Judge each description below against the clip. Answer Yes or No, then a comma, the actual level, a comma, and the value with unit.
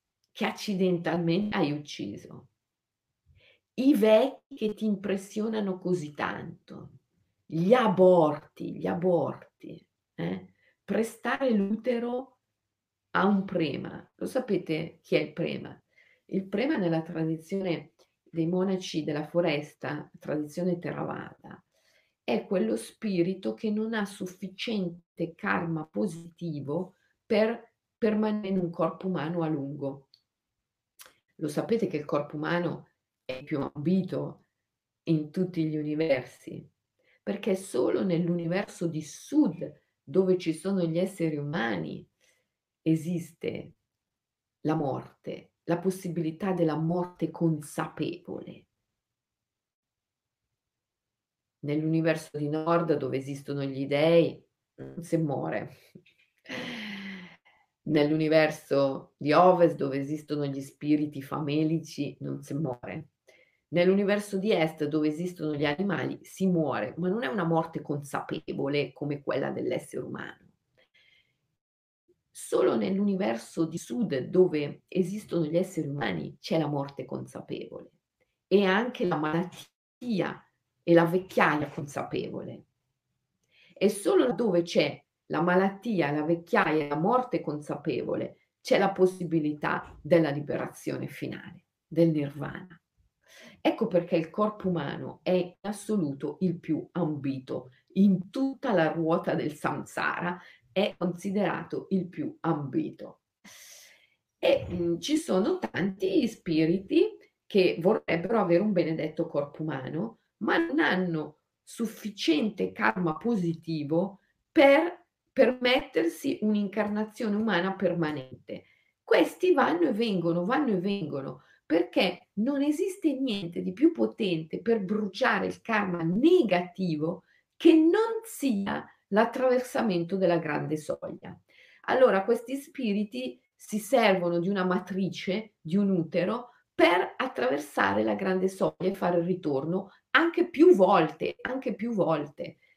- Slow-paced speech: Yes, slow, 110 wpm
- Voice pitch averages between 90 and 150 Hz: No, medium, 175 Hz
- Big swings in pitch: No, average, 4.7 semitones